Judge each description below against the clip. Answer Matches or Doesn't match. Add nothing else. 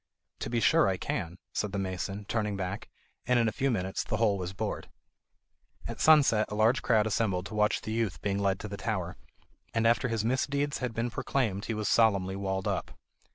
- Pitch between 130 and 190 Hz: Doesn't match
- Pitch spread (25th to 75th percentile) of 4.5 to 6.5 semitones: Doesn't match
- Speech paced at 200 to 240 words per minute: Matches